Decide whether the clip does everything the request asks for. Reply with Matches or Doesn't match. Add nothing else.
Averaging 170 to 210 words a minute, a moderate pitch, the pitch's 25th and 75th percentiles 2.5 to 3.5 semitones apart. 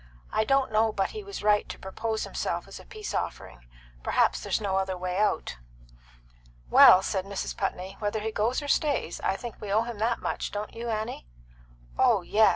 Doesn't match